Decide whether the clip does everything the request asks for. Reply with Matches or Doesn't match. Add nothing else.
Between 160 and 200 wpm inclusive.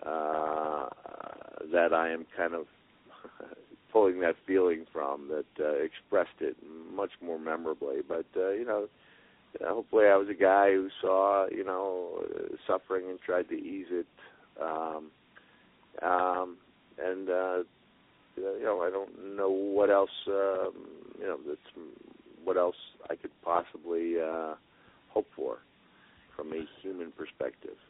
Doesn't match